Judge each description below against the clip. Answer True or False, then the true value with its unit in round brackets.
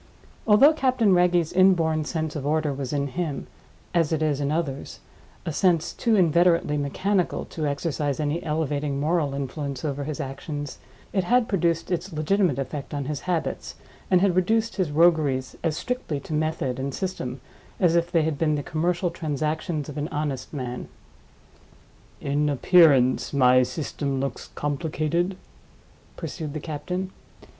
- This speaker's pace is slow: False (150 wpm)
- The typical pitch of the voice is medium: True (155 Hz)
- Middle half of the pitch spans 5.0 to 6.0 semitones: False (3.7 semitones)